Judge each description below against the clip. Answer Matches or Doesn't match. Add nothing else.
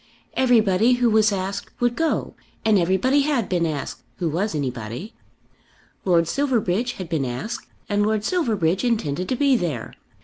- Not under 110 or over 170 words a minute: Matches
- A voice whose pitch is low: Doesn't match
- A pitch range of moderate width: Doesn't match